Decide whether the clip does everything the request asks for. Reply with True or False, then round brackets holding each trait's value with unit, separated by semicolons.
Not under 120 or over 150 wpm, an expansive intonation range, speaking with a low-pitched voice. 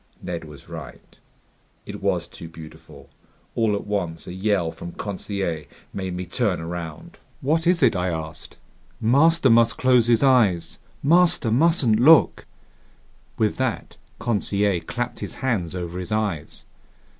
True (140 wpm; 6.1 semitones; 105 Hz)